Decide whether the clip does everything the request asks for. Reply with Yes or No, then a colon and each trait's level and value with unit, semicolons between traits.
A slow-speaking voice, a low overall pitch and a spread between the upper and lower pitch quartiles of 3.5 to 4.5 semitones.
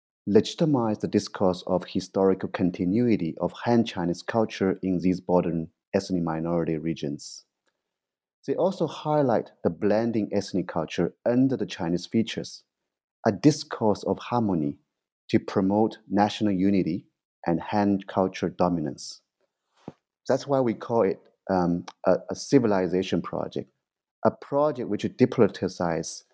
Yes: slow, 120 wpm; low, 100 Hz; average, 4.2 semitones